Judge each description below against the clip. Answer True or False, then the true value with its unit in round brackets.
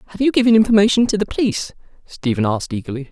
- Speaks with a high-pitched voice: True (195 Hz)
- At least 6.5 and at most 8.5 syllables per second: True (7.7 syllables/s)